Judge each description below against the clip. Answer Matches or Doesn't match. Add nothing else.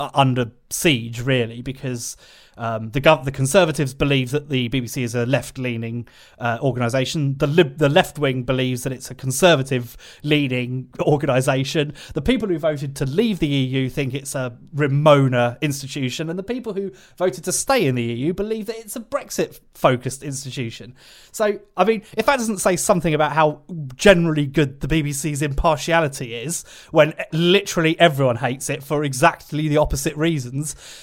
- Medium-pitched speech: Matches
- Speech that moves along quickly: Doesn't match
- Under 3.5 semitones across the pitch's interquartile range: Doesn't match